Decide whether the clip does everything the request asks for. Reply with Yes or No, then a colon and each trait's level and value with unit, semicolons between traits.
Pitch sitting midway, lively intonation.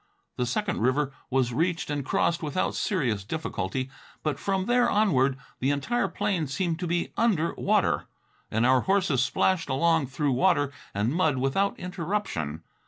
Yes: medium, 155 Hz; wide, 6.0 semitones